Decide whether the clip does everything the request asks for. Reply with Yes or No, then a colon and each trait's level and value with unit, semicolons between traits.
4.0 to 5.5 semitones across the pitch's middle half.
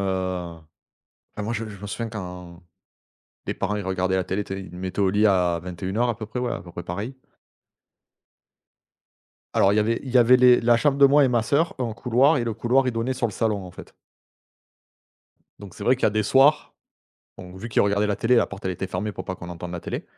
Yes: average, 4.4 semitones